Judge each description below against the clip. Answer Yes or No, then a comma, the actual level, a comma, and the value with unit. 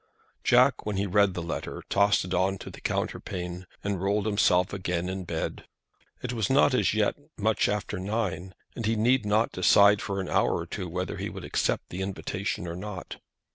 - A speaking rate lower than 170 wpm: No, average, 200 wpm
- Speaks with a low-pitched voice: Yes, low, 100 Hz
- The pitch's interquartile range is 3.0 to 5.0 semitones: No, narrow, 2.5 semitones